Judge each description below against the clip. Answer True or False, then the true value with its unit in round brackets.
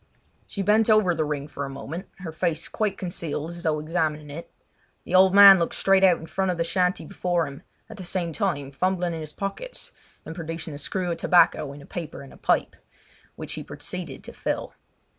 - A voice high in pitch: False (170 Hz)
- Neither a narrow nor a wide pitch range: True (3.5 semitones)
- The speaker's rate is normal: False (215 wpm)